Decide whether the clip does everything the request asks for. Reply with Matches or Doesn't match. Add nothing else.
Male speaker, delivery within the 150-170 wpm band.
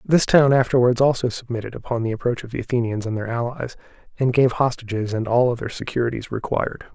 Doesn't match